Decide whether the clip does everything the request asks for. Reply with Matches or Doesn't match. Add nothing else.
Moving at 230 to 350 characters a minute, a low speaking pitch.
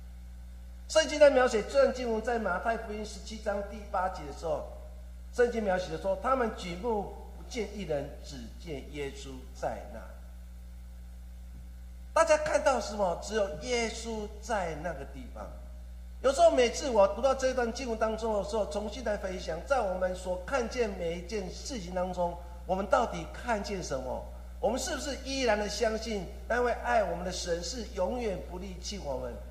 Doesn't match